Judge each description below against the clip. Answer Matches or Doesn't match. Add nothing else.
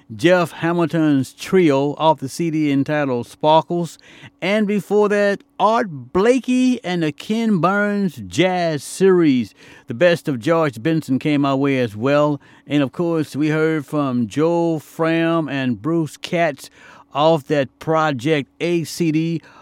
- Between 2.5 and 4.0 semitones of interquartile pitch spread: Matches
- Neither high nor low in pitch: Matches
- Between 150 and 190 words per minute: Doesn't match